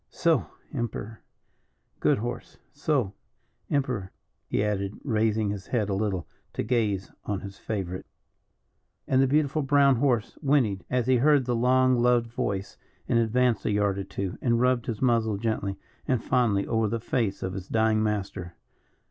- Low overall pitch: Yes, low, 115 Hz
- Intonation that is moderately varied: Yes, average, 3.8 semitones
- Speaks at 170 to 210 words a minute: No, average, 160 wpm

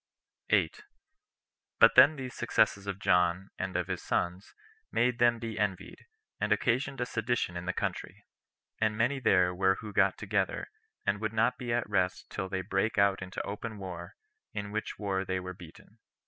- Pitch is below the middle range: Yes, low, 100 Hz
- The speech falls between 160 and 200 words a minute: Yes, average, 175 wpm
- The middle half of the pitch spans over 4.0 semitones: No, average, 3.5 semitones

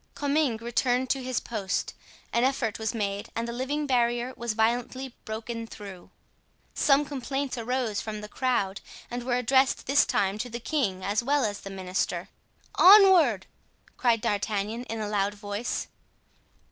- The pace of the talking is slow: No, average, 155 wpm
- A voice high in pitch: Yes, high, 235 Hz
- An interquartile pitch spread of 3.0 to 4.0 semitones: Yes, average, 3.7 semitones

